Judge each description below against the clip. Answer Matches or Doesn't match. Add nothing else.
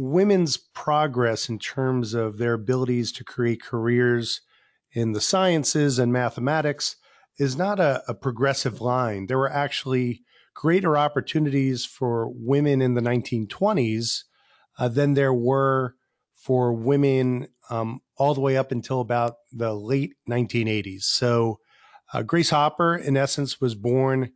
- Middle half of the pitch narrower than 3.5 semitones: Matches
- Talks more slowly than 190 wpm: Matches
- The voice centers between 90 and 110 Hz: Doesn't match